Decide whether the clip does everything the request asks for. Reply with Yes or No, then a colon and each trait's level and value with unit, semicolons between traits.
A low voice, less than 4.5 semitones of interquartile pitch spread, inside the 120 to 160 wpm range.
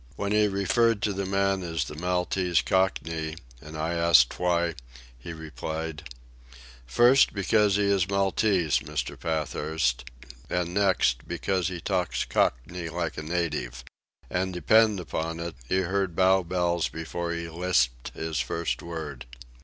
Yes: very low, 85 Hz; average, 3.2 semitones; average, 140 wpm